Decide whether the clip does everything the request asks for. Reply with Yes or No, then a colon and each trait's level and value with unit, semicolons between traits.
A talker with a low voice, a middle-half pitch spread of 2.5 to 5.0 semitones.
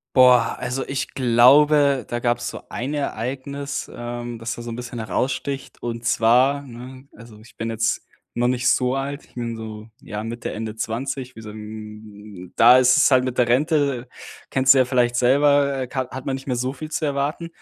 Yes: low, 125 Hz; average, 2.8 semitones